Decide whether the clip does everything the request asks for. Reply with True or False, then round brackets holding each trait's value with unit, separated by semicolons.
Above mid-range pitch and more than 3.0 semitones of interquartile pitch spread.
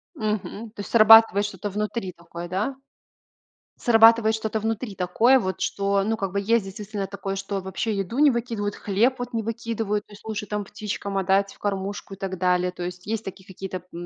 False (205 Hz; 2.5 semitones)